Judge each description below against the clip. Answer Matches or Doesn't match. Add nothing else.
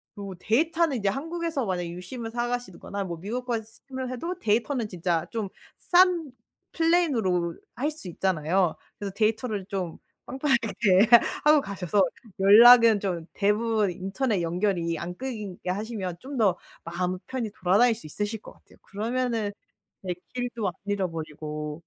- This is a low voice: Doesn't match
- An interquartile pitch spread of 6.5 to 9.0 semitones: Doesn't match